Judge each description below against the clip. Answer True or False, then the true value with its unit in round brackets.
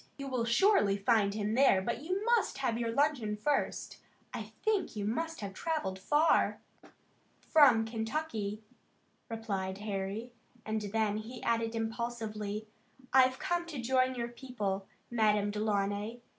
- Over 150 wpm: False (135 wpm)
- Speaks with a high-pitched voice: True (225 Hz)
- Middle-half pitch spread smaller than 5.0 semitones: True (4.0 semitones)